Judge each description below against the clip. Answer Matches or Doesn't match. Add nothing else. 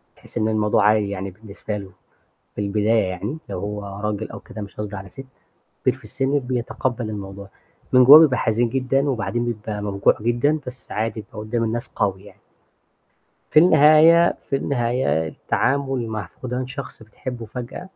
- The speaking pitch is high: Doesn't match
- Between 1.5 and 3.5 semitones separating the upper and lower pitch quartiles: Doesn't match